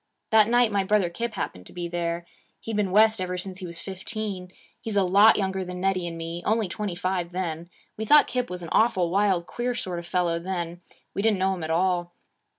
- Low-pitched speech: No, medium, 185 Hz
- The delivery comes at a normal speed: No, fast, 225 wpm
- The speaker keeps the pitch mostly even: No, average, 3.2 semitones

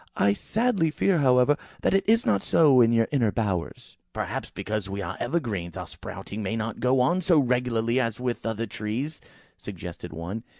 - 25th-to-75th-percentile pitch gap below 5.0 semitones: No, average, 5.3 semitones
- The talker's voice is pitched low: Yes, low, 115 Hz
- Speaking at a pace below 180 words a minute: No, average, 185 wpm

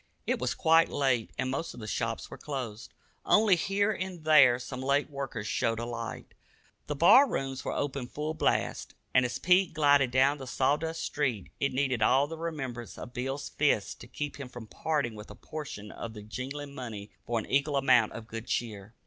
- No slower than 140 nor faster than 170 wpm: No, average, 200 wpm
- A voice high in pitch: No, low, 135 Hz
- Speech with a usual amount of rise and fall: Yes, average, 4.0 semitones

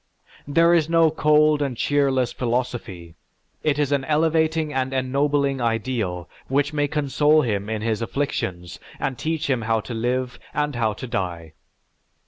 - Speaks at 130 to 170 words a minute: Yes, average, 150 wpm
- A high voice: No, low, 135 Hz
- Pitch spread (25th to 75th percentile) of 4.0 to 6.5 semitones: Yes, average, 4.6 semitones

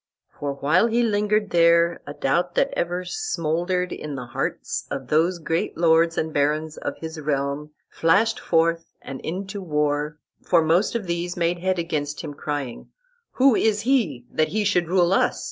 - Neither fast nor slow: Yes, average, 170 wpm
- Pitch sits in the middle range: Yes, medium, 170 Hz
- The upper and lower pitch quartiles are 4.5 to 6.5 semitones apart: No, average, 3.5 semitones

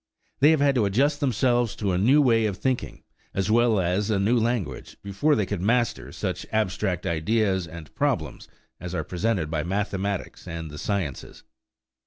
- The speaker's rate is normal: Yes, average, 175 wpm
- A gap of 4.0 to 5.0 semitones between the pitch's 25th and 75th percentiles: Yes, average, 4.7 semitones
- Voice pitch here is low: Yes, low, 100 Hz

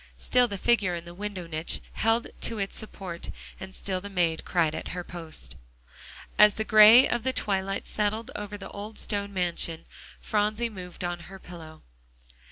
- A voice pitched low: No, high, 195 Hz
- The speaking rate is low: No, average, 175 wpm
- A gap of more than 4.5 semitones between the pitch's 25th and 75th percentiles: No, average, 3.4 semitones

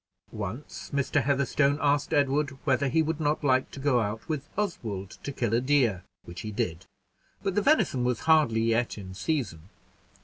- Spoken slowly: No, average, 175 wpm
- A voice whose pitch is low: Yes, low, 130 Hz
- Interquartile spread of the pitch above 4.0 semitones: Yes, average, 4.7 semitones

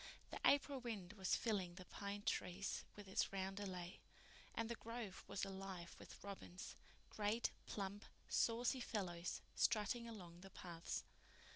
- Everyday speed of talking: No, slow, 130 wpm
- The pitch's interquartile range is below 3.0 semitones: No, average, 3.3 semitones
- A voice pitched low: No, high, 200 Hz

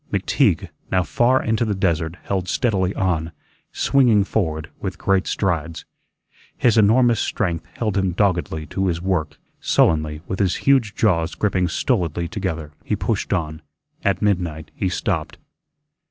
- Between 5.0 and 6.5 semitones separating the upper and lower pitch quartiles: No, average, 4.0 semitones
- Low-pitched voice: Yes, very low, 95 Hz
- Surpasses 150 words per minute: No, average, 140 wpm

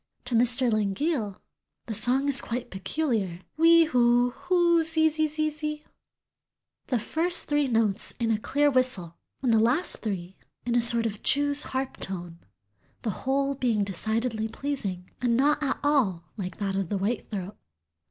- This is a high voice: Yes, high, 240 Hz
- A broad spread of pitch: Yes, wide, 5.7 semitones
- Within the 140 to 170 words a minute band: Yes, average, 160 wpm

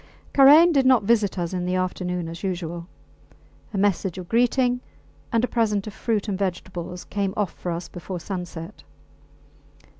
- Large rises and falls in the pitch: No, average, 4.1 semitones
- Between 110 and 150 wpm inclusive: No, average, 160 wpm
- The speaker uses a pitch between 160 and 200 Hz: Yes, high, 190 Hz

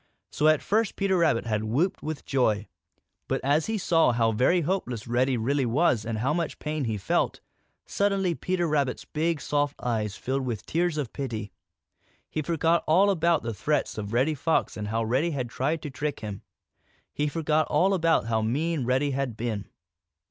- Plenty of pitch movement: Yes, wide, 5.8 semitones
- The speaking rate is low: No, average, 185 wpm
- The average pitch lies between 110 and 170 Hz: Yes, medium, 140 Hz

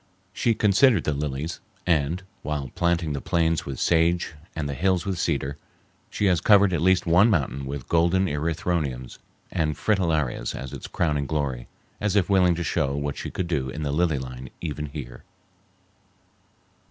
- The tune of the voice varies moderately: Yes, average, 3.9 semitones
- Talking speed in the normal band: Yes, average, 165 wpm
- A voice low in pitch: Yes, very low, 80 Hz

